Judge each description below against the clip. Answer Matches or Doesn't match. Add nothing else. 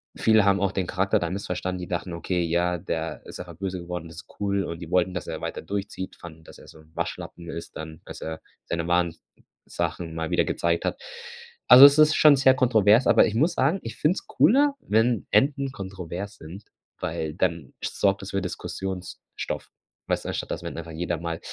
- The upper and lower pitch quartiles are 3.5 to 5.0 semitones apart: Matches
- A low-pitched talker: Matches